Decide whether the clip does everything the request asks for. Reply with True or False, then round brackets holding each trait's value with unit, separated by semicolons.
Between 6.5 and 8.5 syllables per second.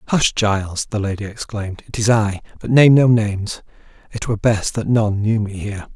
False (5.5 syllables/s)